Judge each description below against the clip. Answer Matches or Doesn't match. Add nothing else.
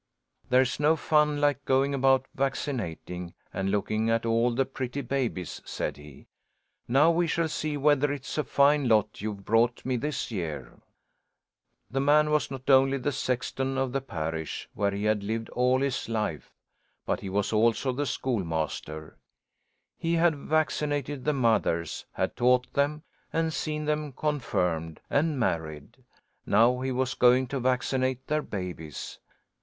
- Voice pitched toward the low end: Matches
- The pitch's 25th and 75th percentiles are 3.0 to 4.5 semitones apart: Doesn't match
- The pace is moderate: Matches